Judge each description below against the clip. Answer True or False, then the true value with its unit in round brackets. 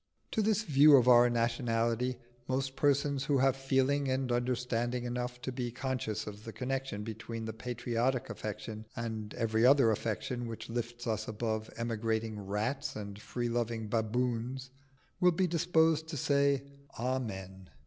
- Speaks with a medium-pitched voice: False (120 Hz)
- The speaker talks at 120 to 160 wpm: True (150 wpm)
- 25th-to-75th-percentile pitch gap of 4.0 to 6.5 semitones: False (3.0 semitones)